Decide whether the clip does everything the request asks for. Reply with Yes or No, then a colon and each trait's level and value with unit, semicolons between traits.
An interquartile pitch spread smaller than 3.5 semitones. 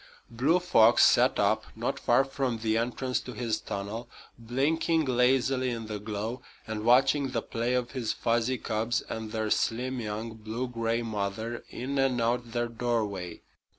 Yes: narrow, 2.4 semitones